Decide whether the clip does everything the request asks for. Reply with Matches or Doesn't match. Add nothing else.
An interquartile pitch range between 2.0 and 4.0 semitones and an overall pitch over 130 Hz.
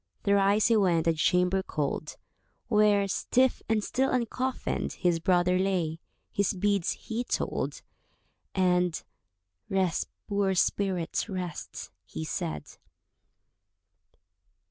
Matches